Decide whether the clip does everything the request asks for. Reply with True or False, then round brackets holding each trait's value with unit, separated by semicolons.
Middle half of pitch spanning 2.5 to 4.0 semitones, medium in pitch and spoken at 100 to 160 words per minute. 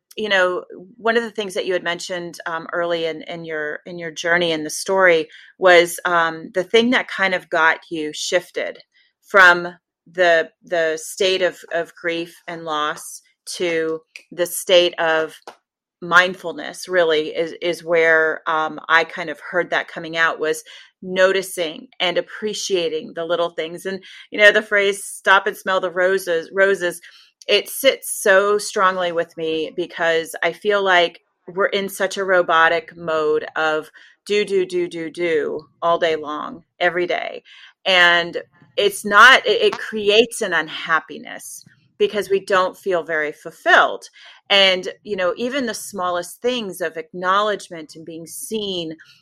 True (3.0 semitones; 175 Hz; 155 wpm)